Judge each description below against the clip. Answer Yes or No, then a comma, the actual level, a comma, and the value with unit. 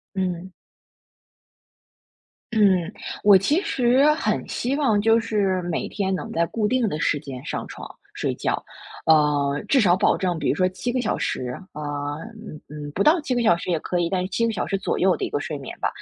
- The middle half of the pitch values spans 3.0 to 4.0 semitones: No, wide, 5.4 semitones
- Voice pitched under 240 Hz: Yes, high, 190 Hz